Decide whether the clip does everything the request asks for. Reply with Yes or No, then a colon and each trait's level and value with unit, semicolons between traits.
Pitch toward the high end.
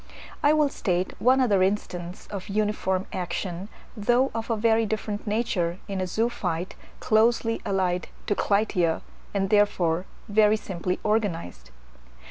Yes: high, 205 Hz